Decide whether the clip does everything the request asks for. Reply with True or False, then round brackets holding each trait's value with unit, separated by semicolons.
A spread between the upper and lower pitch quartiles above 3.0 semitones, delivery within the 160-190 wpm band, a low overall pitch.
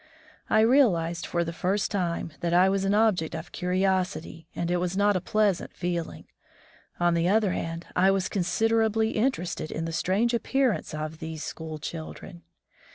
False (3.7 semitones; 170 wpm; 180 Hz)